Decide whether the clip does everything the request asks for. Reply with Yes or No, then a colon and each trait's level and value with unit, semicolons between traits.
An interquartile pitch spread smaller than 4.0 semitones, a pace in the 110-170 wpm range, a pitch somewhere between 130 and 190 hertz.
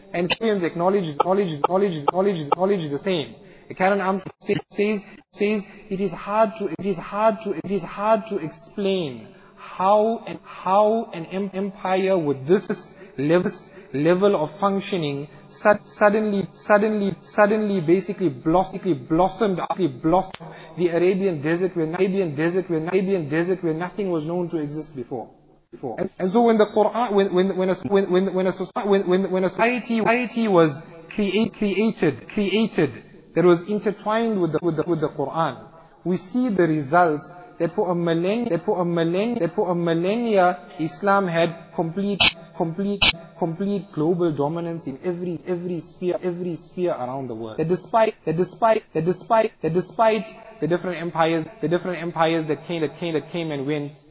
Yes: average, 3.3 semitones; average, 160 wpm; medium, 185 Hz